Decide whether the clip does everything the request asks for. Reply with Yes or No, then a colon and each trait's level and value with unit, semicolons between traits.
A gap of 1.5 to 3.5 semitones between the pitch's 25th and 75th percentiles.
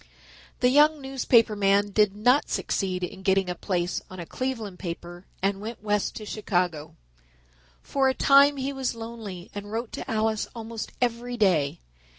No: average, 4.4 semitones